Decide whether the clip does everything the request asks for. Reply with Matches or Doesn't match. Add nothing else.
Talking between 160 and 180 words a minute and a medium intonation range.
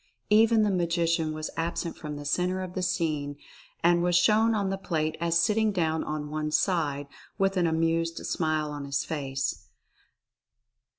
Matches